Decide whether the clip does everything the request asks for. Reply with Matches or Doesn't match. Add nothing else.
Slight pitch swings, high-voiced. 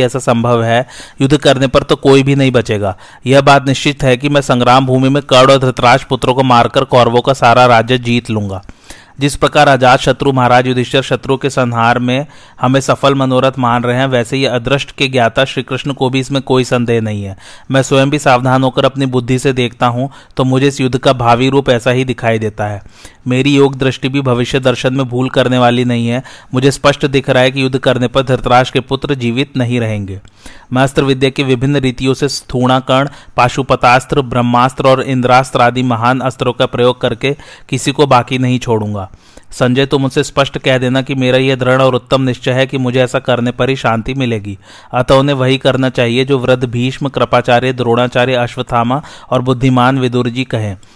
Doesn't match